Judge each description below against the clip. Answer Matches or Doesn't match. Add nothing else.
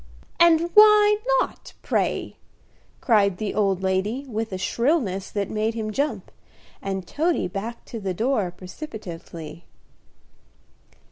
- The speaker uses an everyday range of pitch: Doesn't match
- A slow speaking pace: Matches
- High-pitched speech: Matches